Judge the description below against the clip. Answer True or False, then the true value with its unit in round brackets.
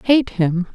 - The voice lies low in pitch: False (205 Hz)